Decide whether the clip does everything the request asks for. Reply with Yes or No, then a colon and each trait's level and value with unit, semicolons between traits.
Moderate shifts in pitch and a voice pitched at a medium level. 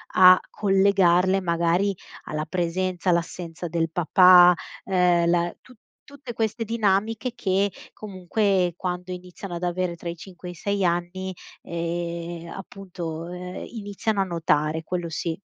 No: narrow, 2.2 semitones; medium, 180 Hz